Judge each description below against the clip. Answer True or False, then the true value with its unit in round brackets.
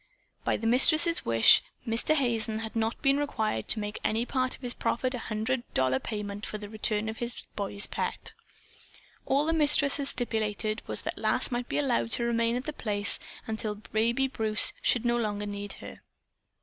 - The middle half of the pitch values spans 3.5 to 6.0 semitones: False (3.0 semitones)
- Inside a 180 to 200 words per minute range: True (185 wpm)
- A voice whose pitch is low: False (225 Hz)